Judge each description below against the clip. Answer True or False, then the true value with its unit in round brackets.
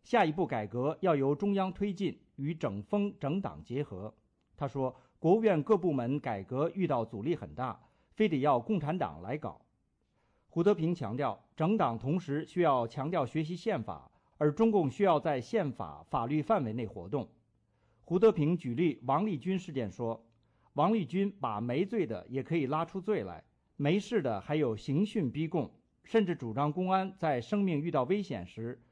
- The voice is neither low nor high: True (150 Hz)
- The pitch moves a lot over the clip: True (7.6 semitones)